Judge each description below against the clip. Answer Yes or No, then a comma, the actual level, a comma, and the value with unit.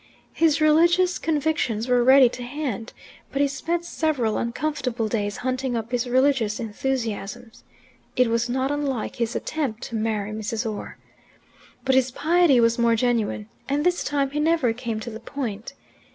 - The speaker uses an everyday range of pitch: Yes, average, 4.1 semitones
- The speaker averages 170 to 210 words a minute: No, average, 160 wpm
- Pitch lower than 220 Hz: No, very high, 250 Hz